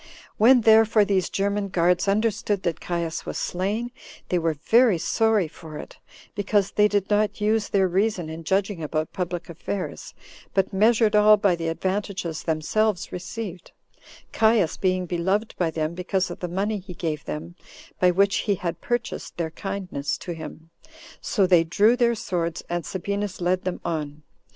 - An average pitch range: Yes, average, 3.5 semitones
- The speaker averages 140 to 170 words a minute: Yes, average, 165 wpm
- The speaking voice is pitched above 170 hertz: Yes, high, 190 Hz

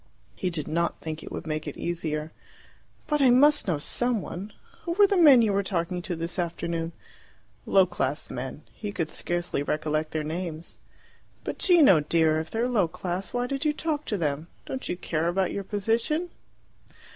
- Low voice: No, medium, 180 Hz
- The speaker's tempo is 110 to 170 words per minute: No, average, 185 wpm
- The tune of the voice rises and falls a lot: Yes, wide, 7.1 semitones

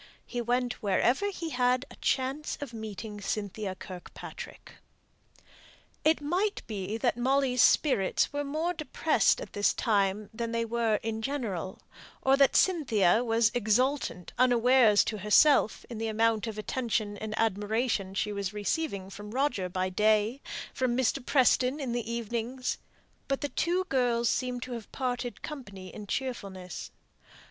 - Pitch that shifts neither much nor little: Yes, average, 3.9 semitones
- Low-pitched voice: No, high, 235 Hz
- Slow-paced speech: No, average, 145 wpm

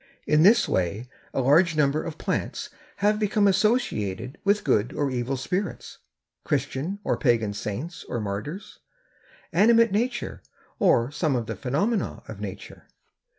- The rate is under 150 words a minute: Yes, average, 140 wpm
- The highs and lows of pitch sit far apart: Yes, wide, 8.8 semitones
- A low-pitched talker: No, medium, 150 Hz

